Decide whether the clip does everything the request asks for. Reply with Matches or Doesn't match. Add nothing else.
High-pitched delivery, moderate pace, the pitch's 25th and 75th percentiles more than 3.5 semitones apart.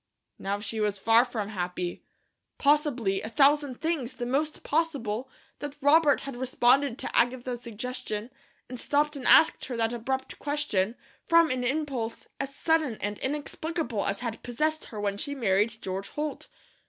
Matches